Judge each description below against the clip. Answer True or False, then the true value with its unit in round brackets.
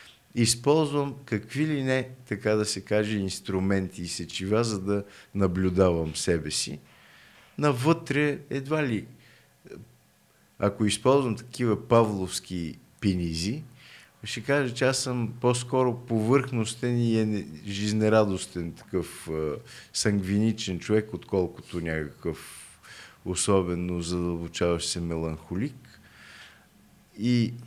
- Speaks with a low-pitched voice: True (105 Hz)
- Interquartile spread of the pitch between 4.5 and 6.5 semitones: True (5.1 semitones)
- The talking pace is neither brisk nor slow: False (100 wpm)